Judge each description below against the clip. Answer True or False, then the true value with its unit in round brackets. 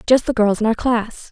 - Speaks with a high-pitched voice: True (230 Hz)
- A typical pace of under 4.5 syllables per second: False (5.2 syllables/s)